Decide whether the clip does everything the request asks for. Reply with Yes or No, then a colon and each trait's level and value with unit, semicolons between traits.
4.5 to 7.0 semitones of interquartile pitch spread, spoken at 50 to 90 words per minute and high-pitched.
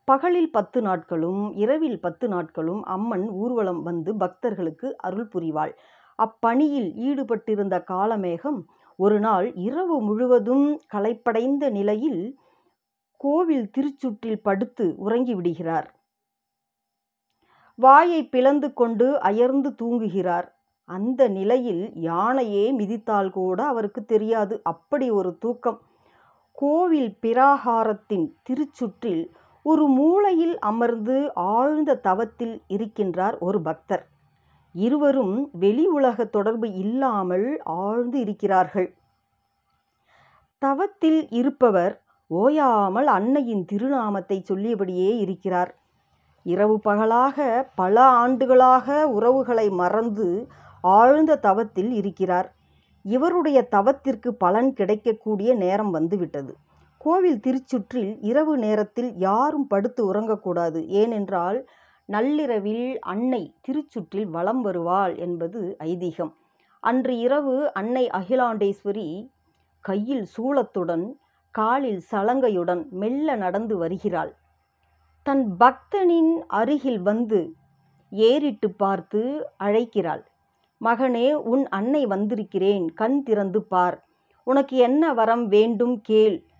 Yes: average, 5.2 semitones; average, 85 wpm; high, 225 Hz